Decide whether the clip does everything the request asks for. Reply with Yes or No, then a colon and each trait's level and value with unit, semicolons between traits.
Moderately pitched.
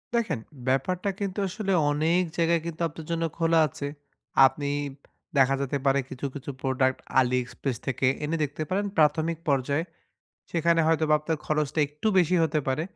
Yes: medium, 155 Hz